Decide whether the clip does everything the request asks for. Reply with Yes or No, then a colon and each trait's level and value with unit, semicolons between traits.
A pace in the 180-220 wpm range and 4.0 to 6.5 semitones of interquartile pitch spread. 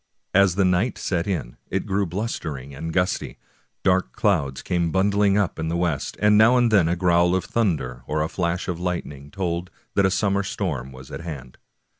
No: average, 195 wpm; average, 3.6 semitones